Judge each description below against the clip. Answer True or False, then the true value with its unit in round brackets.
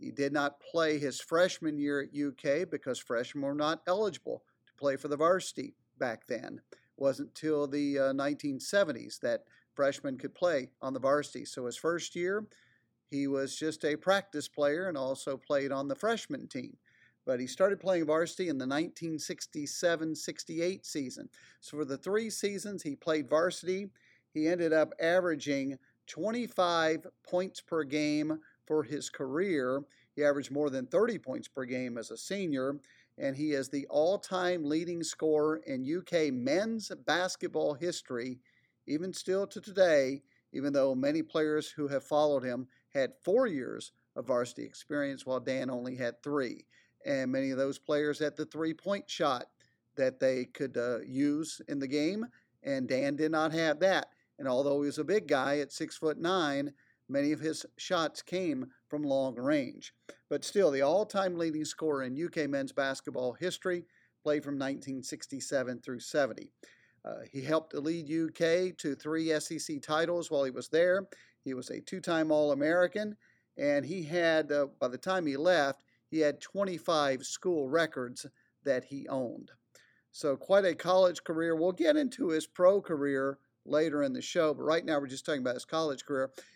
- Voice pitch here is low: False (155 Hz)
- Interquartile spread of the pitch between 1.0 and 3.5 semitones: False (4.6 semitones)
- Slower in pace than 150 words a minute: False (170 wpm)